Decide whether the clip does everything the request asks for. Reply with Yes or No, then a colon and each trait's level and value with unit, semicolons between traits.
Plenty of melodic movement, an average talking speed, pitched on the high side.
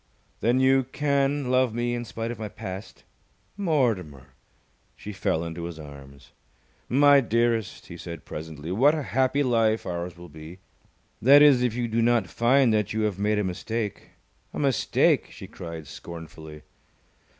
No: wide, 6.9 semitones; average, 160 wpm; low, 110 Hz